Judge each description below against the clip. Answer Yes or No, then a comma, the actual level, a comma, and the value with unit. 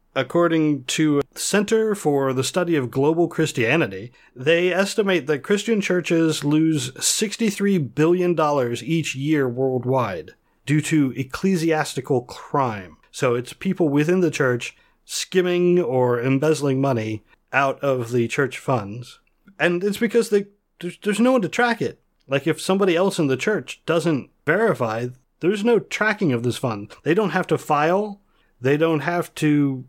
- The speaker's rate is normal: Yes, average, 150 wpm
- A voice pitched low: No, medium, 155 Hz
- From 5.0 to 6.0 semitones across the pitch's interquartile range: Yes, wide, 5.5 semitones